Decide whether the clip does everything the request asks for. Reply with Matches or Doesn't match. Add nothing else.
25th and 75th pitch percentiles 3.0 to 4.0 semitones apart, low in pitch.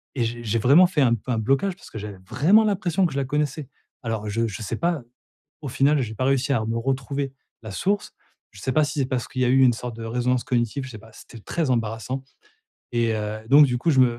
Matches